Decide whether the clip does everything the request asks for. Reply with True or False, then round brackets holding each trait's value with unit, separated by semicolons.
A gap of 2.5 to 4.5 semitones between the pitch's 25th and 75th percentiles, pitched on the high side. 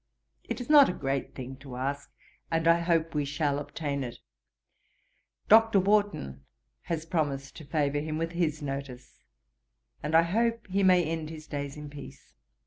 False (3.5 semitones; 155 Hz)